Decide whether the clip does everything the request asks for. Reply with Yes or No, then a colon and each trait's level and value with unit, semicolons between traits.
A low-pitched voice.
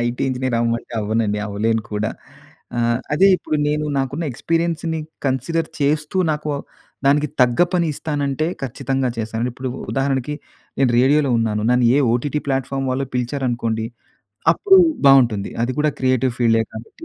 Yes: low, 130 Hz